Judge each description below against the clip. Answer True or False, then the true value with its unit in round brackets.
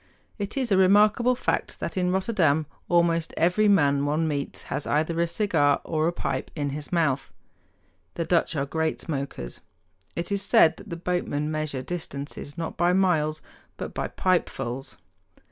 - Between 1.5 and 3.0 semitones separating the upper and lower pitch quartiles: False (4.0 semitones)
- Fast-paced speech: False (160 wpm)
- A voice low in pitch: False (165 Hz)